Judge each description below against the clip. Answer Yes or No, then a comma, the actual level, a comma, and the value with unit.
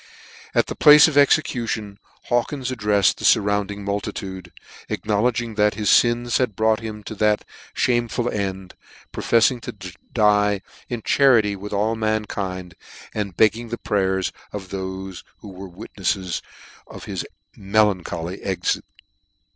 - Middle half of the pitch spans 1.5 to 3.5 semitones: Yes, average, 3.0 semitones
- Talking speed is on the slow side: Yes, slow, 130 wpm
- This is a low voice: Yes, low, 105 Hz